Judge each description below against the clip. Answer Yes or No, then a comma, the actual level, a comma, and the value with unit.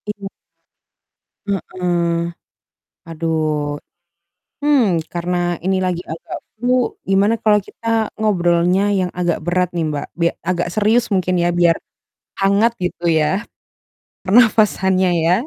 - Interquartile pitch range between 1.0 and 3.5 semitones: Yes, average, 3.2 semitones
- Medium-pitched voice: Yes, medium, 180 Hz